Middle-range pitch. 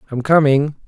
Yes: medium, 145 Hz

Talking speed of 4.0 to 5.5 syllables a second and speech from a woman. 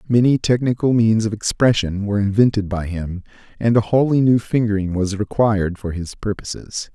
No: 5.3 syllables/s; male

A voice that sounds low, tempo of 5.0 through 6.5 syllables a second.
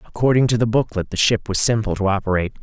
No: low, 110 Hz; 7.1 syllables/s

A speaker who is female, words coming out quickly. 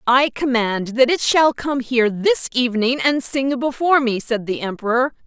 No: female; average, 180 wpm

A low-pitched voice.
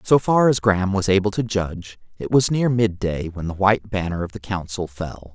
Yes: low, 100 Hz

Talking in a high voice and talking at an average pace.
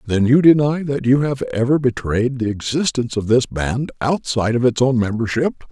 No: low, 125 Hz; average, 190 wpm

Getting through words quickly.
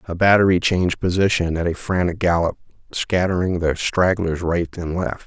No: average, 160 wpm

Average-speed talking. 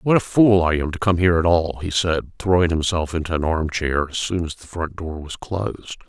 No: fast, 255 wpm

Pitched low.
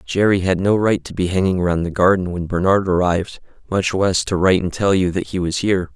Yes: very low, 95 Hz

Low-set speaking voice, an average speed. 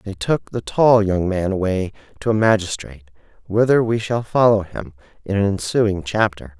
Yes: low, 100 Hz; average, 175 wpm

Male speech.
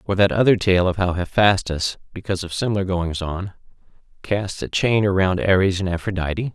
Yes: male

